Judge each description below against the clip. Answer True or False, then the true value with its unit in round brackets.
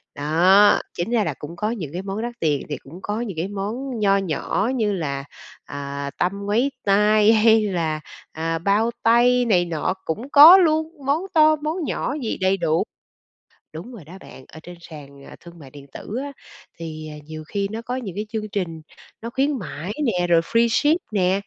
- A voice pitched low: False (200 Hz)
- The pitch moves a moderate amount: False (6.0 semitones)